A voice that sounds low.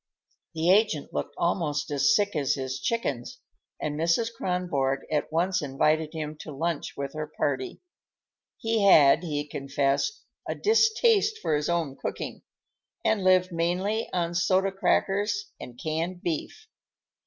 No: medium, 165 Hz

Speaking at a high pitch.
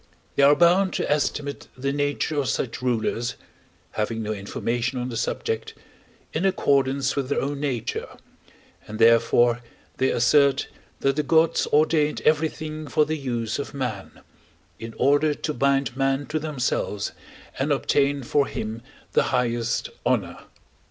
No: low, 135 Hz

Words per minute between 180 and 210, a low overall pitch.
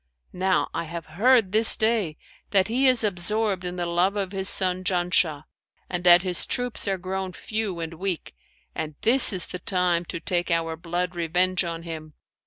No: average, 185 wpm; medium, 180 Hz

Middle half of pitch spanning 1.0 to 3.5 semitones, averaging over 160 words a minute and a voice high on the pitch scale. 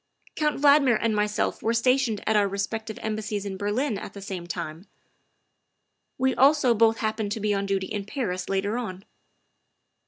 Yes: average, 2.9 semitones; average, 175 wpm; high, 215 Hz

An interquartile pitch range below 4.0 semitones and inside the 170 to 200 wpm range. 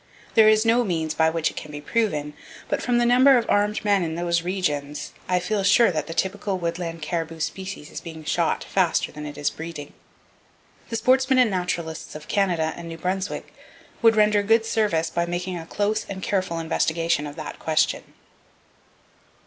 No: average, 4.6 semitones; average, 185 wpm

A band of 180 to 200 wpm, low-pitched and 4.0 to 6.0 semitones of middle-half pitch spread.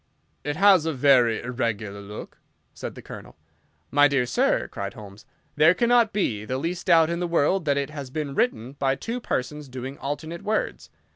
No: average, 185 wpm; medium, 145 Hz; average, 5.1 semitones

